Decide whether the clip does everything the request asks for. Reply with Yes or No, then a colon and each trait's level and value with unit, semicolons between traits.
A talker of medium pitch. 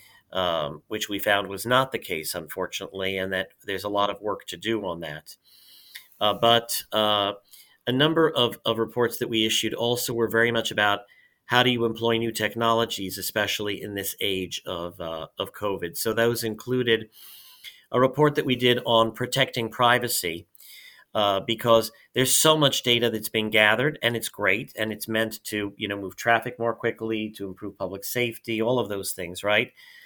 No: low, 115 Hz